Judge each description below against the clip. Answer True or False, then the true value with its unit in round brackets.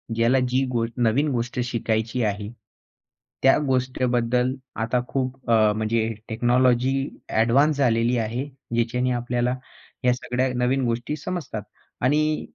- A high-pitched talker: False (125 Hz)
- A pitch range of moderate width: False (2.0 semitones)